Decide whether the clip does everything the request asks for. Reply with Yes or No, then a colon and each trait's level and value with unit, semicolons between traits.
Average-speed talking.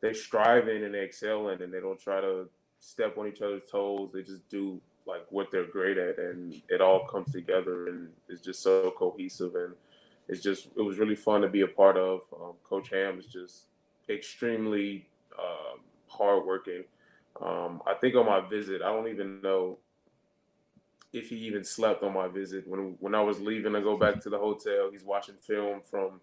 Yes: average, 195 wpm